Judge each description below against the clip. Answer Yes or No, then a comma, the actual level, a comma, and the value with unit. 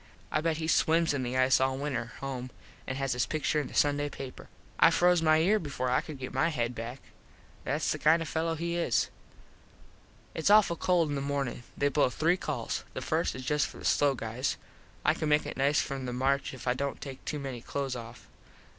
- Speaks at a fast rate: Yes, fast, 225 wpm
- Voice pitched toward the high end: No, medium, 140 Hz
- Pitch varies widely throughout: No, average, 3.5 semitones